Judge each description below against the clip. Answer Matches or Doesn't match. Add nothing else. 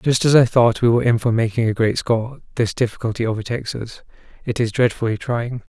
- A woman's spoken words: Doesn't match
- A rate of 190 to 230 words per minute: Matches